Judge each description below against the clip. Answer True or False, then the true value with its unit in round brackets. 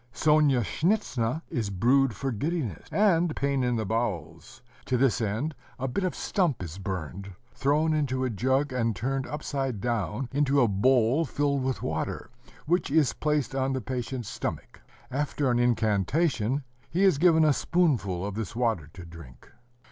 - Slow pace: False (160 wpm)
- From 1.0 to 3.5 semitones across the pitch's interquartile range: False (5.0 semitones)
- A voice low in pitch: True (130 Hz)